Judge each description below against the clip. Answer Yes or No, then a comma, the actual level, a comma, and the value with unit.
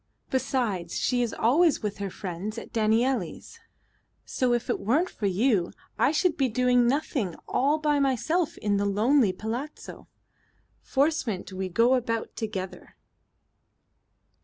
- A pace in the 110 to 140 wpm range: Yes, slow, 135 wpm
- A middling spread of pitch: Yes, average, 5.0 semitones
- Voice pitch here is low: No, high, 235 Hz